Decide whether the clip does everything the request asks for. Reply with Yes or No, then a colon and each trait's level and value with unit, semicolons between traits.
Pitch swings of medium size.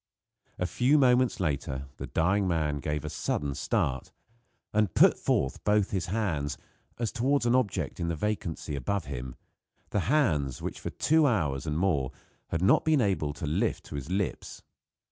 No: wide, 6.5 semitones